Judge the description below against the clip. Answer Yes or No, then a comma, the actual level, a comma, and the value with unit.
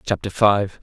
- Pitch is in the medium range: No, very low, 95 Hz